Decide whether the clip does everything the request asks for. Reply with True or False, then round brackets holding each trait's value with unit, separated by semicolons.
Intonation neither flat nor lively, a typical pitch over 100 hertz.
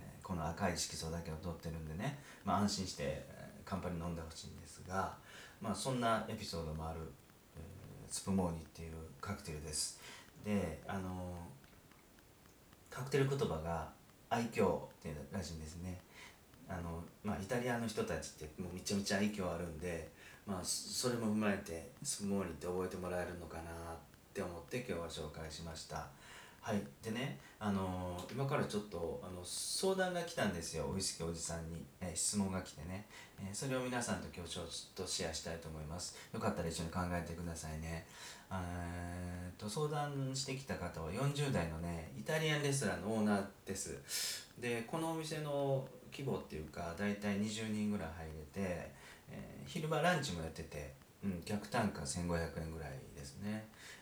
False (4.1 semitones; 90 Hz)